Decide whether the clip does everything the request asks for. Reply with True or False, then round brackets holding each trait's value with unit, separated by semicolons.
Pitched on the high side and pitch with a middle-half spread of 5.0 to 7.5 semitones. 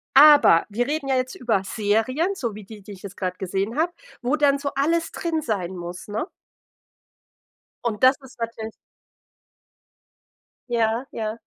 True (235 Hz; 5.3 semitones)